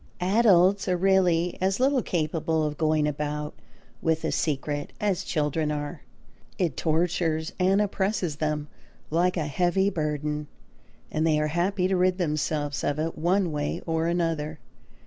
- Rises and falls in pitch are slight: No, average, 3.3 semitones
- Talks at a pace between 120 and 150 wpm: Yes, average, 145 wpm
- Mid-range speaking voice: Yes, medium, 165 Hz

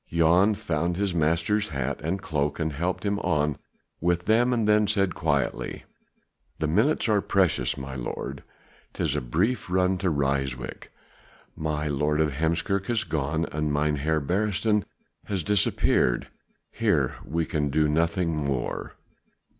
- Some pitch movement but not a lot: Yes, average, 4.7 semitones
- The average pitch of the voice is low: Yes, very low, 80 Hz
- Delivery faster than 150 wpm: No, average, 145 wpm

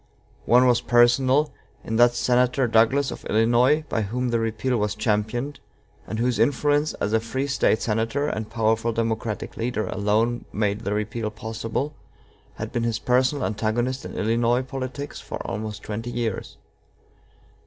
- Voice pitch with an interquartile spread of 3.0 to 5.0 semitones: No, narrow, 2.5 semitones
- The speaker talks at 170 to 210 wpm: No, average, 150 wpm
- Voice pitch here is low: Yes, low, 115 Hz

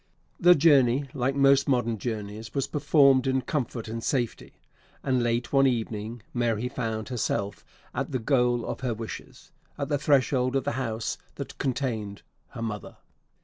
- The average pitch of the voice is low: Yes, low, 125 Hz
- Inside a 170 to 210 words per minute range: No, average, 155 wpm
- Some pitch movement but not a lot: Yes, average, 3.2 semitones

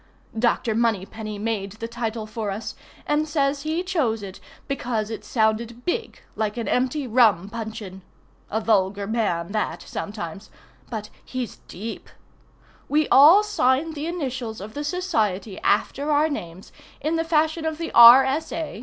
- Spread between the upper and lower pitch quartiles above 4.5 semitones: Yes, wide, 5.6 semitones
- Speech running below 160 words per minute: Yes, average, 150 wpm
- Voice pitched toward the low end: No, high, 230 Hz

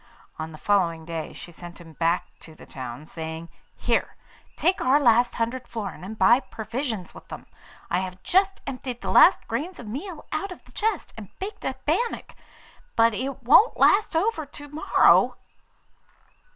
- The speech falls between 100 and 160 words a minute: No, average, 170 wpm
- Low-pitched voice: No, high, 230 Hz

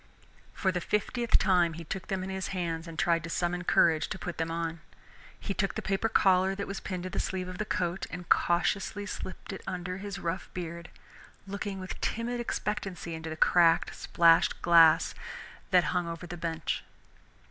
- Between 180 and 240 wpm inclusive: Yes, average, 190 wpm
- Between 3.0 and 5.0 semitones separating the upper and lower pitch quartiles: No, narrow, 2.4 semitones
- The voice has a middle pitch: Yes, medium, 180 Hz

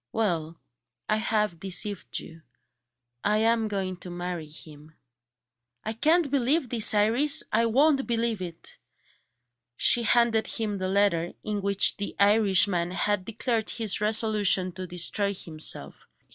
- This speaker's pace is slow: Yes, slow, 130 wpm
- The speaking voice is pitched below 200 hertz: No, high, 205 Hz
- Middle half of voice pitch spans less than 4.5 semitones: Yes, average, 3.7 semitones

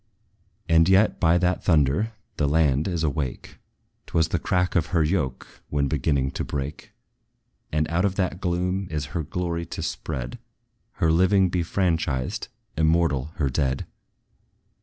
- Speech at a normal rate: Yes, average, 150 wpm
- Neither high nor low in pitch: No, very low, 80 Hz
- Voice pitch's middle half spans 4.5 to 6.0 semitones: No, average, 3.9 semitones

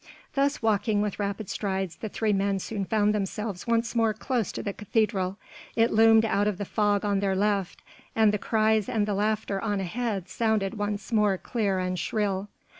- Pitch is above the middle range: Yes, high, 210 Hz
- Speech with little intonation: Yes, narrow, 2.0 semitones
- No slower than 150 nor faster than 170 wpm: No, average, 190 wpm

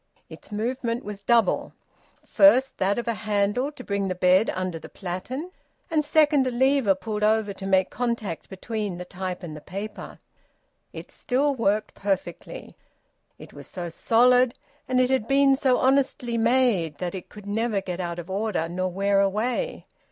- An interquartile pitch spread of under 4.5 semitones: No, average, 4.9 semitones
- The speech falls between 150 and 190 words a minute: Yes, average, 170 wpm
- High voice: Yes, high, 210 Hz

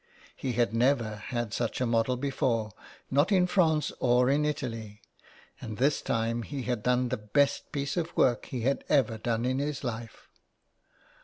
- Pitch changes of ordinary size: Yes, average, 3.5 semitones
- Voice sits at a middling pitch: No, low, 125 Hz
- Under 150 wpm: No, average, 170 wpm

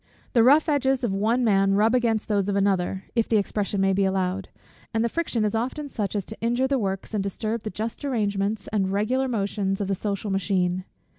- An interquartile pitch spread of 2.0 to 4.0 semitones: Yes, average, 3.1 semitones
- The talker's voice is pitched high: Yes, high, 210 Hz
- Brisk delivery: Yes, fast, 215 wpm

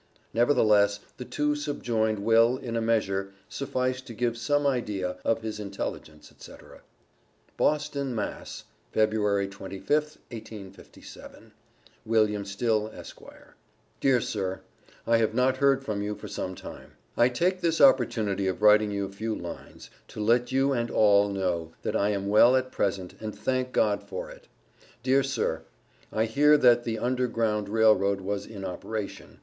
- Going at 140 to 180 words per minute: Yes, average, 155 wpm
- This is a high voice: No, low, 110 Hz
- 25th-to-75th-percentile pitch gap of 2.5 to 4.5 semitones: Yes, average, 4.0 semitones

